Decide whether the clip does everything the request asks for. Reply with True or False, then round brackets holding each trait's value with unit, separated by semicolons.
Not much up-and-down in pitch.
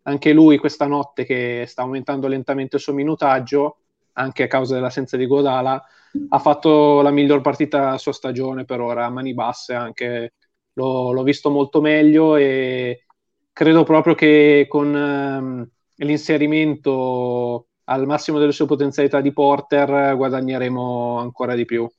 True (2.3 semitones)